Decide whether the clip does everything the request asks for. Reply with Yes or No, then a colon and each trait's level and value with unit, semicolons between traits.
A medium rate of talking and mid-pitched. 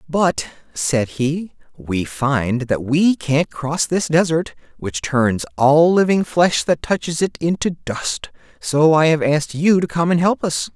Yes: average, 175 wpm; medium, 150 Hz